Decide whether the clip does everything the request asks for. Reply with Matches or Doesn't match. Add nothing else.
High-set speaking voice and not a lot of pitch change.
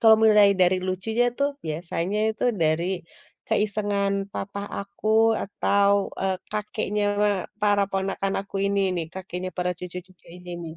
Matches